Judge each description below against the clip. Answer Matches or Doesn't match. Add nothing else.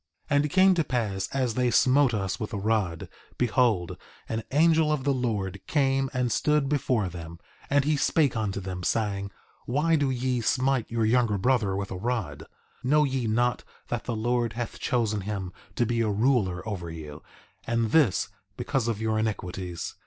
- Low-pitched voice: Matches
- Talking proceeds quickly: Doesn't match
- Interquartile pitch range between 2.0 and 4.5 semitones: Doesn't match